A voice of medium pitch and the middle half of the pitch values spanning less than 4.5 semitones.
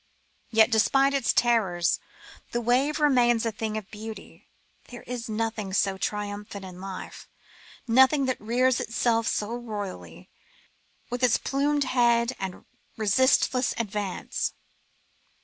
No: high, 230 Hz; average, 3.2 semitones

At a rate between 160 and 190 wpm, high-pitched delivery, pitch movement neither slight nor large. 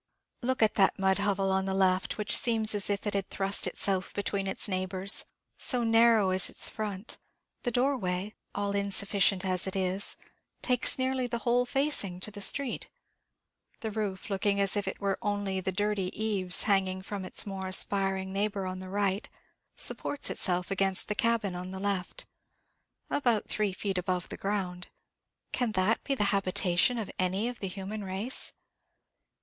No: average, 170 wpm; high, 200 Hz; narrow, 2.2 semitones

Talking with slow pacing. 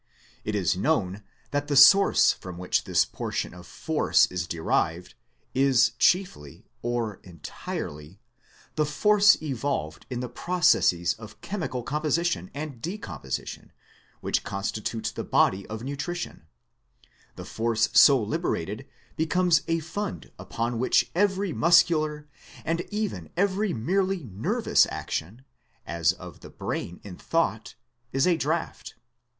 Yes: slow, 125 wpm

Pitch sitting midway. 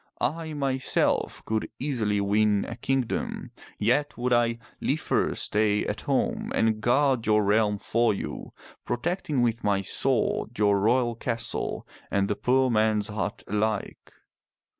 No: low, 115 Hz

